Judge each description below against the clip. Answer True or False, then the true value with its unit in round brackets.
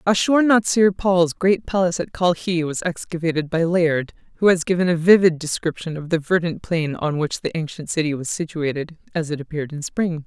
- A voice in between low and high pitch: True (170 Hz)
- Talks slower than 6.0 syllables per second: True (5.4 syllables/s)